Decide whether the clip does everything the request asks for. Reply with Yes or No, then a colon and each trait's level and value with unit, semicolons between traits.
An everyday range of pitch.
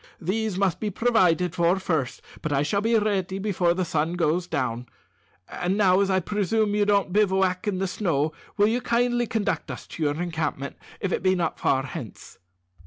Yes: average, 3.8 semitones